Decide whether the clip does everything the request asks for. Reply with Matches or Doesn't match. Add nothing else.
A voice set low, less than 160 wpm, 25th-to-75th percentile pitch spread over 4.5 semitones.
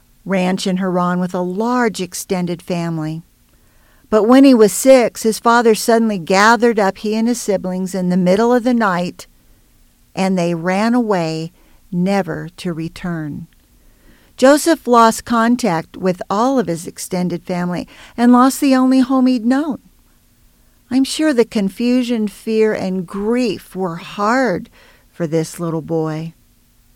Doesn't match